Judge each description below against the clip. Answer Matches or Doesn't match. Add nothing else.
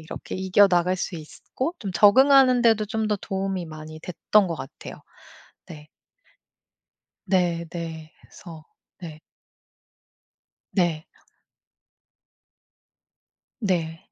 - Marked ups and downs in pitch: Doesn't match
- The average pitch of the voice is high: Doesn't match